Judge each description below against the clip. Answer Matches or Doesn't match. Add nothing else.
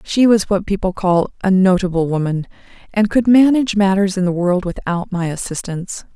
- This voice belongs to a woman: Matches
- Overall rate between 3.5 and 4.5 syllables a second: Doesn't match